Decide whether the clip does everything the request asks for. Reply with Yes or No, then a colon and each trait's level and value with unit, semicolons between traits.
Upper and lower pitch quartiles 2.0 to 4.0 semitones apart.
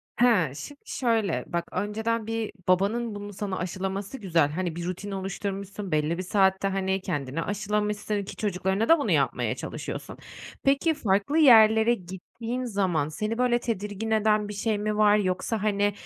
Yes: average, 2.8 semitones